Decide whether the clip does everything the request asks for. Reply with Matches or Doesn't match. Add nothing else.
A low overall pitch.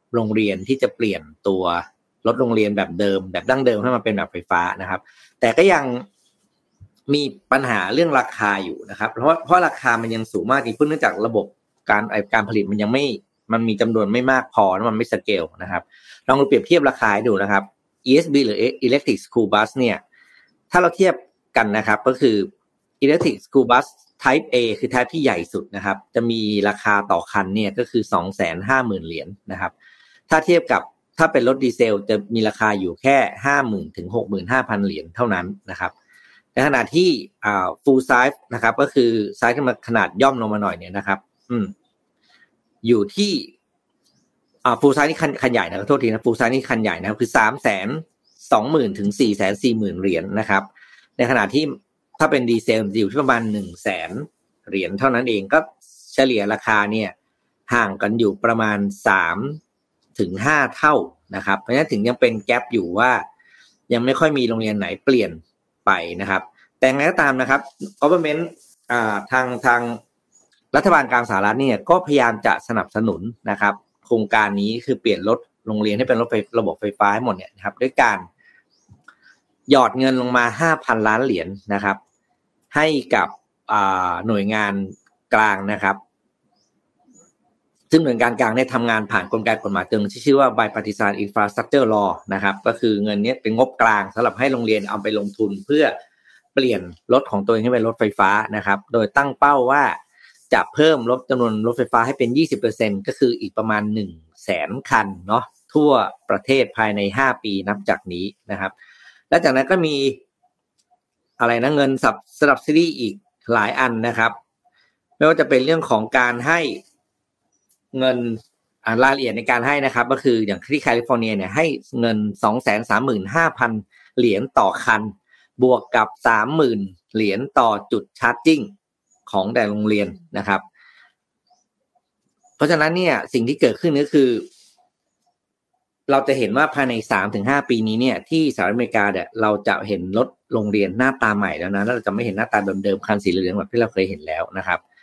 Matches